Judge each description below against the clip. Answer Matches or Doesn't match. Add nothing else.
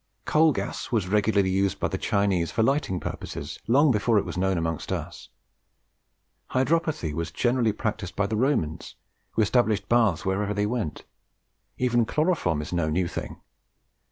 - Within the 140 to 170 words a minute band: Matches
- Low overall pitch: Matches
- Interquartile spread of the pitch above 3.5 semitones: Matches